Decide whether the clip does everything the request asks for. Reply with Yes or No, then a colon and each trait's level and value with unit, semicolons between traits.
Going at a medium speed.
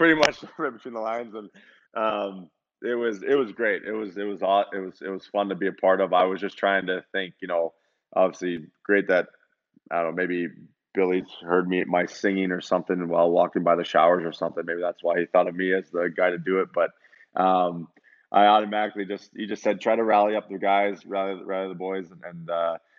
No: fast, 235 wpm